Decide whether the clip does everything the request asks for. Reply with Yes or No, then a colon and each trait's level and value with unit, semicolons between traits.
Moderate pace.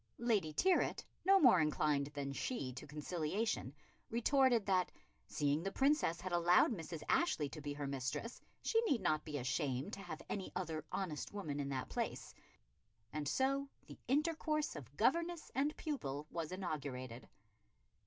Yes: average, 155 wpm